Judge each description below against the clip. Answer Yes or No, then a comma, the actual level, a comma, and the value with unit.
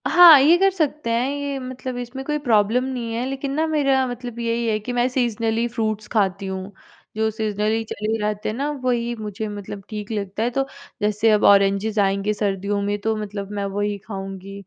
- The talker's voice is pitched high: Yes, high, 220 Hz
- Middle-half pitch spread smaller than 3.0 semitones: No, average, 3.4 semitones